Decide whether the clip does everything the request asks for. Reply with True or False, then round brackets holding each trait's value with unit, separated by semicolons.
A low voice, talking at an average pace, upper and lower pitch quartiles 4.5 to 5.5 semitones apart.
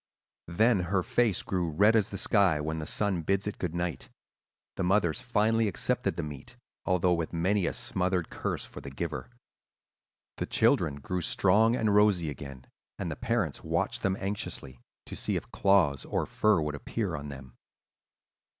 True (90 Hz; 170 wpm; 4.9 semitones)